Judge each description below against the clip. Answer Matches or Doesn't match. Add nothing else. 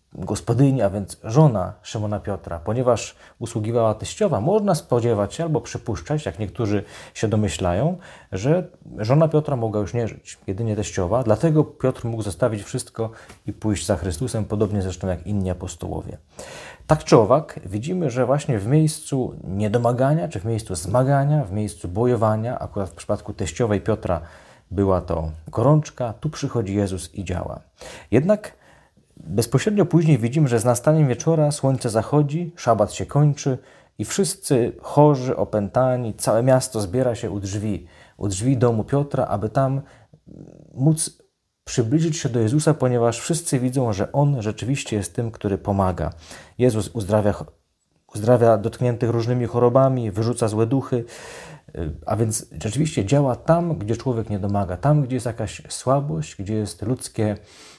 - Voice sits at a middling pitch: Doesn't match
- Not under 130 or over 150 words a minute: Matches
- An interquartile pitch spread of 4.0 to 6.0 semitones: Matches